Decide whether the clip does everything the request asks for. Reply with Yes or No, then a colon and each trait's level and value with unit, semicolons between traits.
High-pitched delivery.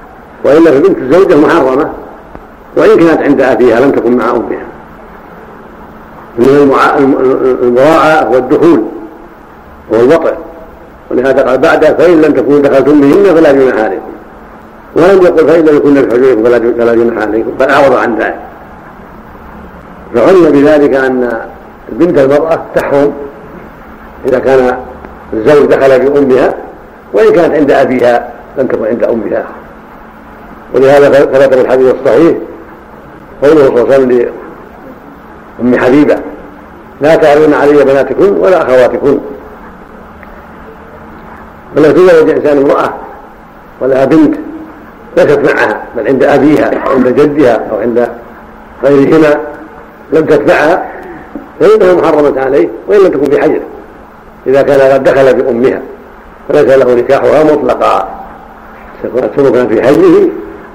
No: medium, 140 Hz